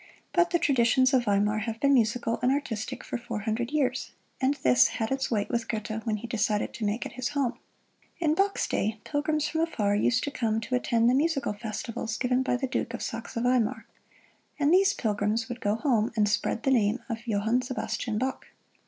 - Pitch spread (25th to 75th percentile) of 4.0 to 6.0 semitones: No, average, 3.6 semitones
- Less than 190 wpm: No, fast, 205 wpm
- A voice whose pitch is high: Yes, high, 235 Hz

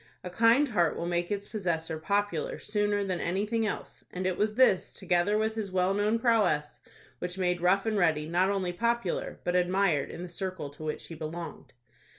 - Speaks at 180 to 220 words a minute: Yes, average, 190 wpm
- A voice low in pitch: No, medium, 185 Hz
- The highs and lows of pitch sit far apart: No, average, 3.1 semitones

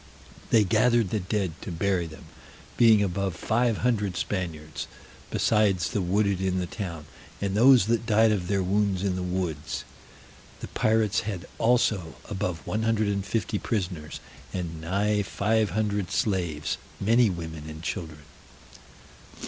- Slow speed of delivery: No, average, 145 wpm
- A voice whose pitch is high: No, low, 100 Hz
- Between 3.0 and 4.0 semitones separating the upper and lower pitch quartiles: Yes, average, 3.5 semitones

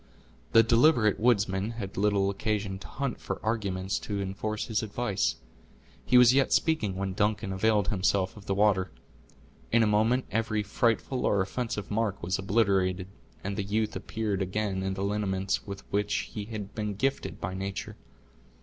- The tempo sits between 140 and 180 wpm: Yes, average, 165 wpm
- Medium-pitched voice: No, low, 105 Hz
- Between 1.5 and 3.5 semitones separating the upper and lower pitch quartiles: Yes, narrow, 2.4 semitones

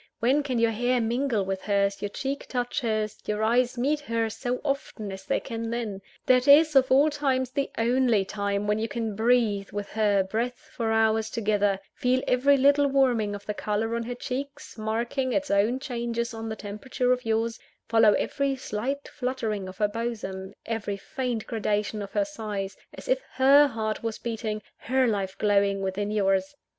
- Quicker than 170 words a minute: Yes, average, 185 wpm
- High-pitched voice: Yes, high, 225 Hz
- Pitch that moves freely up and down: No, average, 3.5 semitones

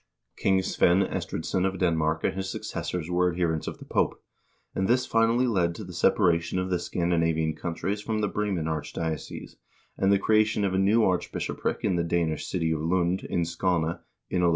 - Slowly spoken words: No, average, 195 wpm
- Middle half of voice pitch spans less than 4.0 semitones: Yes, narrow, 2.6 semitones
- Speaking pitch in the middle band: No, very low, 90 Hz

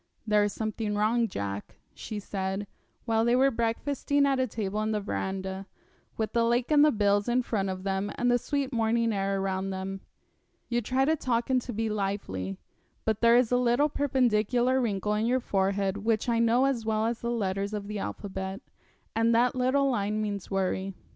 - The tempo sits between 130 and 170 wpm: No, average, 195 wpm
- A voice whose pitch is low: No, high, 220 Hz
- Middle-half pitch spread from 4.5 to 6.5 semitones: No, average, 3.6 semitones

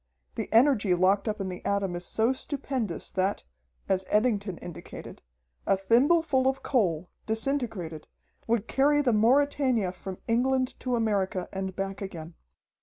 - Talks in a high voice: Yes, high, 215 Hz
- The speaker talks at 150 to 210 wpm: No, average, 140 wpm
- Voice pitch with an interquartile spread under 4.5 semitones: No, average, 5.3 semitones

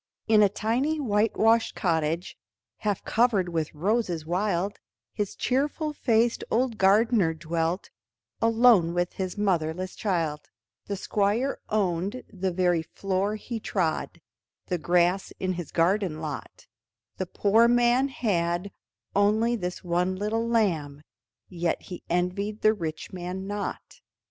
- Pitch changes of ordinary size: Yes, average, 4.2 semitones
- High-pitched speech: Yes, high, 195 Hz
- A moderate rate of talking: No, slow, 125 wpm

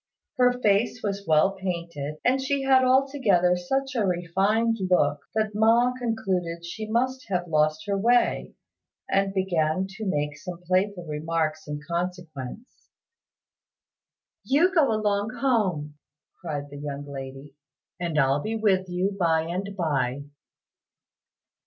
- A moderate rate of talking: No, slow, 130 wpm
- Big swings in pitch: Yes, wide, 5.9 semitones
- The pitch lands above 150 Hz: Yes, medium, 185 Hz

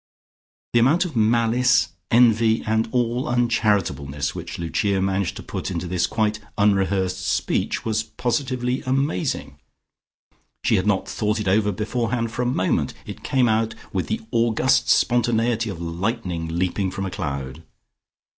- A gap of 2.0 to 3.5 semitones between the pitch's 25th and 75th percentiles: No, average, 4.1 semitones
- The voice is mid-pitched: No, low, 110 Hz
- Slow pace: No, average, 145 wpm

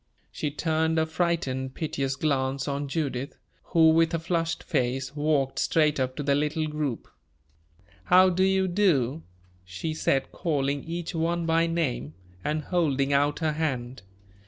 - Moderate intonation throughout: Yes, average, 3.3 semitones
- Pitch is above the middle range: No, medium, 150 Hz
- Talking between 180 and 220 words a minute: No, average, 150 wpm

